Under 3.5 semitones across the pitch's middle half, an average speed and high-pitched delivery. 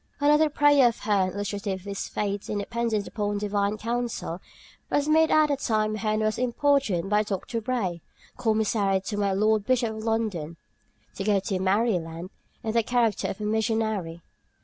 Yes: average, 2.9 semitones; average, 170 wpm; high, 215 Hz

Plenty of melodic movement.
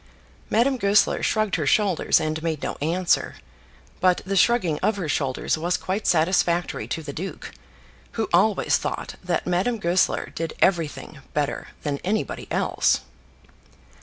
No: average, 4.0 semitones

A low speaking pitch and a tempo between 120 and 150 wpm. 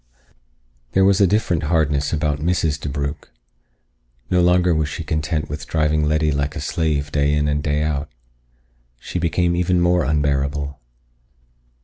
Yes: very low, 75 Hz; average, 145 wpm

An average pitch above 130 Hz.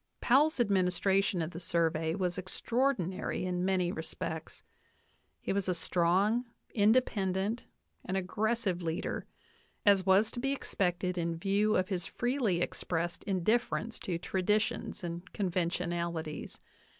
Yes: medium, 185 Hz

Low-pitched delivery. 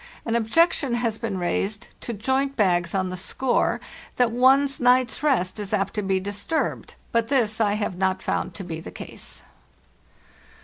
No: high, 220 Hz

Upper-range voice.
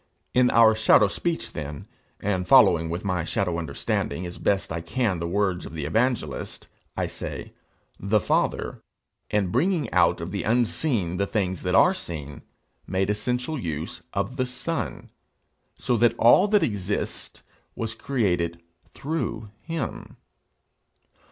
No: low, 100 Hz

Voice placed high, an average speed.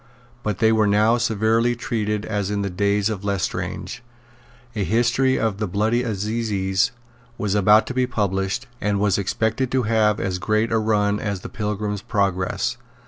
No: low, 105 Hz; average, 170 wpm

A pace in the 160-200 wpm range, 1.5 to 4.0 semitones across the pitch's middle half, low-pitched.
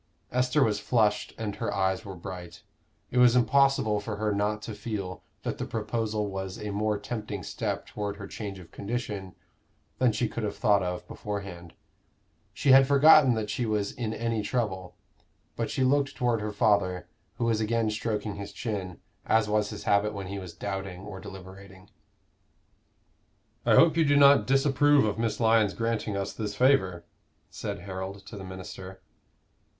Yes: average, 170 wpm; average, 2.9 semitones; low, 105 Hz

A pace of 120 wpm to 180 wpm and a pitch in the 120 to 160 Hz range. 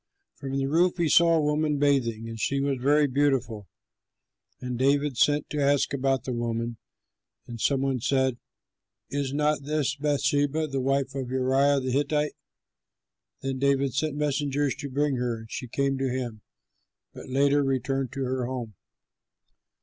Yes: average, 160 wpm; low, 135 Hz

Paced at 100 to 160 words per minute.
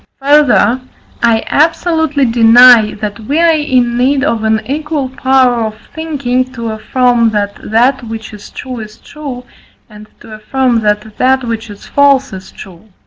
Yes: average, 155 wpm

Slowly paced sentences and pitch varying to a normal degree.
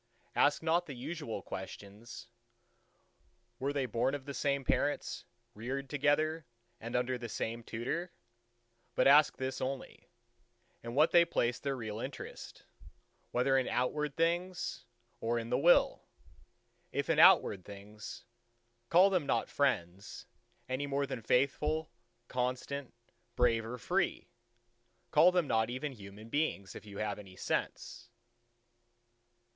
Yes: slow, 130 wpm; average, 4.2 semitones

